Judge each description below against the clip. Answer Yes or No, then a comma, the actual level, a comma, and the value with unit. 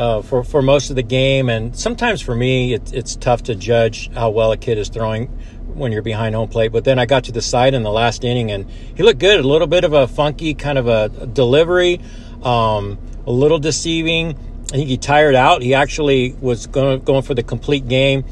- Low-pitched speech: Yes, low, 125 Hz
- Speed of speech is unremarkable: No, fast, 230 wpm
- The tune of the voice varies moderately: Yes, average, 3.8 semitones